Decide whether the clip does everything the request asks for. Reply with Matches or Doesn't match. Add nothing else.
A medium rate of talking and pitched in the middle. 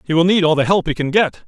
Doesn't match